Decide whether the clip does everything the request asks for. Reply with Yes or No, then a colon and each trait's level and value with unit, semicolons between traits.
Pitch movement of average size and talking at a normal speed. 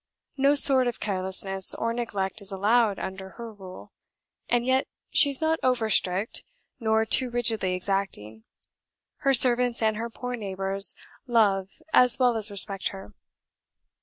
Yes: average, 4.0 semitones; average, 145 wpm